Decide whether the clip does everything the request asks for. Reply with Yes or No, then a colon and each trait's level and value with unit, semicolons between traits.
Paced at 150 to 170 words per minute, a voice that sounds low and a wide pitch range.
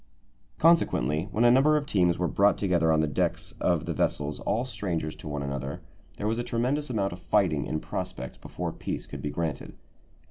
No: average, 200 wpm; very low, 90 Hz; wide, 7.6 semitones